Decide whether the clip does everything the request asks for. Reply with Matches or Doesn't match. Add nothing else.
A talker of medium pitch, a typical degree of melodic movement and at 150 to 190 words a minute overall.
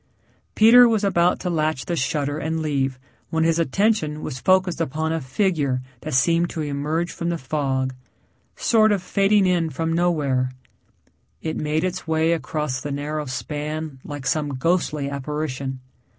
Matches